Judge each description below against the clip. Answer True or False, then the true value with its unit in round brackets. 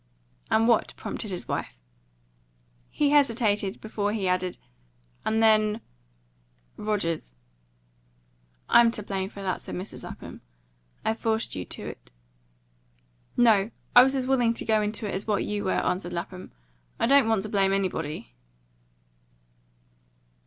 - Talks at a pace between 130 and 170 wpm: True (140 wpm)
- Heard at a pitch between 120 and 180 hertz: False (210 Hz)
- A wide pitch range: False (2.9 semitones)